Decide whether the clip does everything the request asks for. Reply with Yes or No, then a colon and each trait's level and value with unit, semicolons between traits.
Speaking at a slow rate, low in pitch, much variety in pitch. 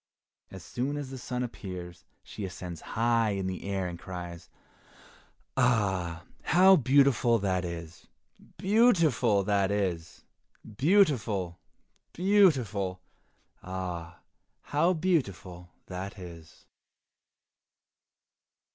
Yes: slow, 95 wpm; low, 100 Hz; wide, 6.8 semitones